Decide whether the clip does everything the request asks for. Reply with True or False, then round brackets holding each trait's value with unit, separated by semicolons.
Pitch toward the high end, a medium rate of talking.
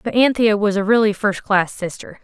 True (210 Hz; 190 wpm)